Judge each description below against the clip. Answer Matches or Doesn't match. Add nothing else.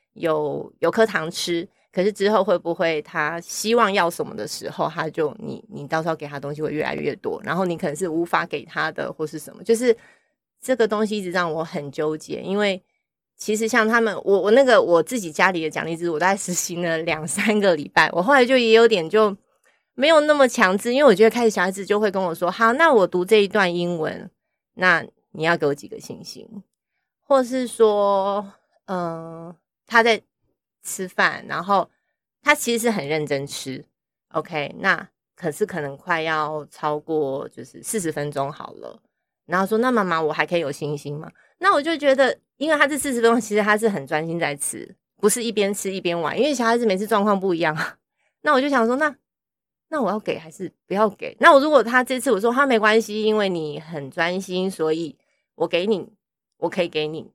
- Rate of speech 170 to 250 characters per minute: Doesn't match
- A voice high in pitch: Matches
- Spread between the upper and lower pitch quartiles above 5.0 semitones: Matches